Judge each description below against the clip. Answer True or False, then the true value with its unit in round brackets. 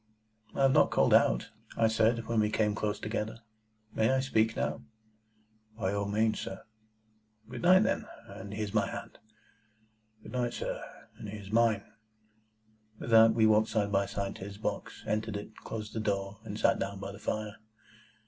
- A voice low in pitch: True (110 Hz)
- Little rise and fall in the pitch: True (1.8 semitones)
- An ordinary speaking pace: True (175 wpm)